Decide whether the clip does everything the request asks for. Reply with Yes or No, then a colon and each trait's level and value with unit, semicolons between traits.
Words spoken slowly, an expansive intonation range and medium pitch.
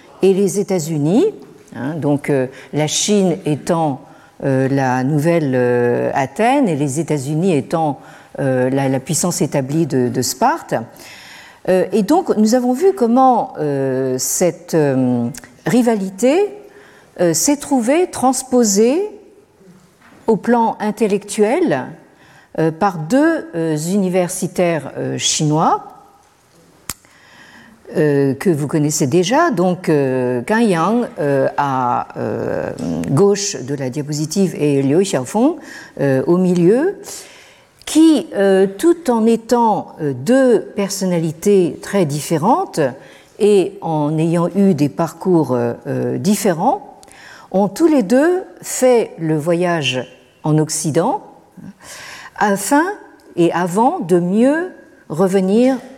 Yes: slow, 110 wpm; wide, 8.0 semitones; medium, 180 Hz